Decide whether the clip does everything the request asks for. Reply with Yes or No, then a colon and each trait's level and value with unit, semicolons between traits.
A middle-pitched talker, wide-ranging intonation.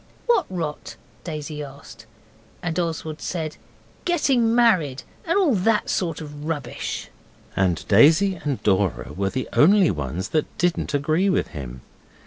Yes: medium, 155 Hz; wide, 6.3 semitones